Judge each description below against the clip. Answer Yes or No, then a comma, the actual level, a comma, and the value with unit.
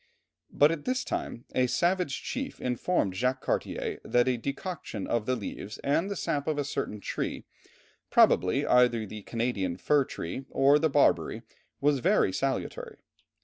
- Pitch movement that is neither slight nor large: Yes, average, 4.1 semitones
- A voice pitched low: Yes, low, 130 Hz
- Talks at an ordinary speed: Yes, average, 150 wpm